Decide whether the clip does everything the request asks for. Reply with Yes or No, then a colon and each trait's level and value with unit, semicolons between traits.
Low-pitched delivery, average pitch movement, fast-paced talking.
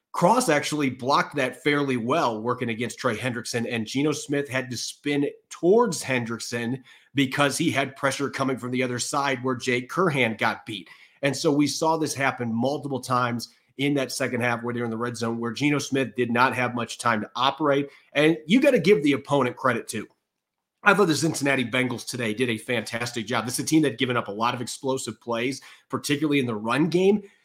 Yes: low, 130 Hz; average, 3.1 semitones; fast, 210 wpm